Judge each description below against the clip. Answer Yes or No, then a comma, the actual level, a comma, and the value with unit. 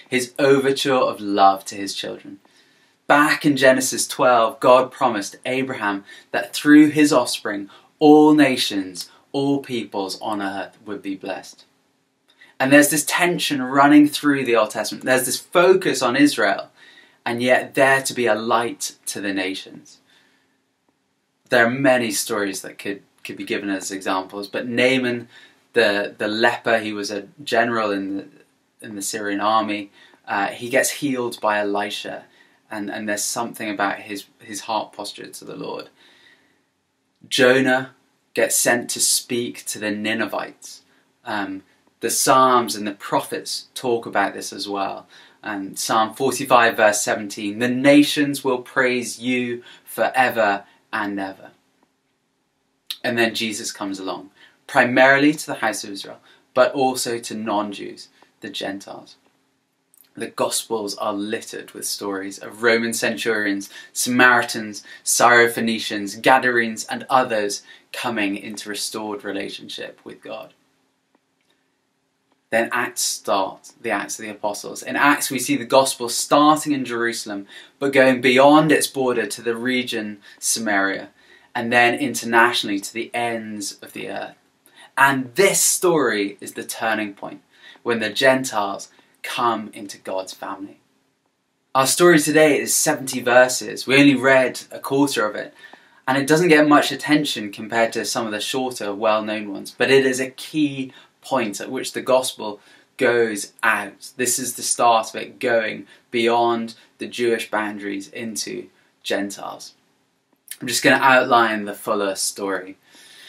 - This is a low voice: Yes, low, 120 Hz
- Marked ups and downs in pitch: No, average, 4.3 semitones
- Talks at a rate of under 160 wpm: Yes, average, 145 wpm